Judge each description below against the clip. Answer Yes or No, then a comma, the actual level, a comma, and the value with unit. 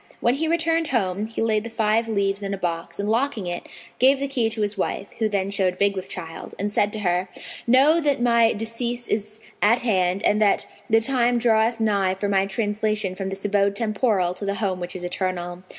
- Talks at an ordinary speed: No, fast, 215 wpm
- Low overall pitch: No, high, 210 Hz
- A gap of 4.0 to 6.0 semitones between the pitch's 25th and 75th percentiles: No, average, 3.2 semitones